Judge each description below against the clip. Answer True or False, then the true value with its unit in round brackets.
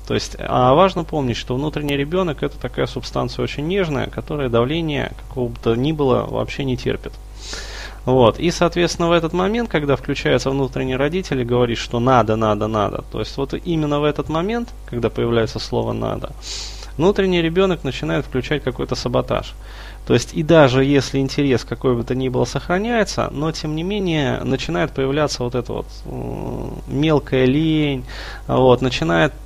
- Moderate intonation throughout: True (4.3 semitones)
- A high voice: False (135 Hz)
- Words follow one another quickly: True (165 wpm)